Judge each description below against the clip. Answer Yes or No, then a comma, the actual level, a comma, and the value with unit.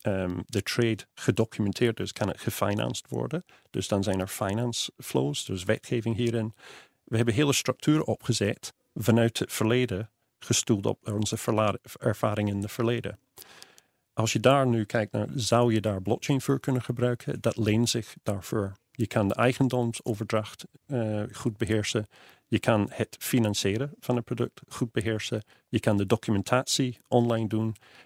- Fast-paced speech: No, average, 155 wpm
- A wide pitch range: No, narrow, 2.6 semitones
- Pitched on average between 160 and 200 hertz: No, low, 115 Hz